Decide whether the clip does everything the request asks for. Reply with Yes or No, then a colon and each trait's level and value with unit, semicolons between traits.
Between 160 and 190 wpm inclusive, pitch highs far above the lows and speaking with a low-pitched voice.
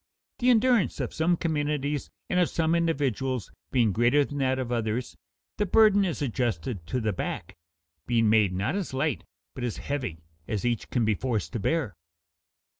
Yes: average, 175 wpm; wide, 6.0 semitones; low, 130 Hz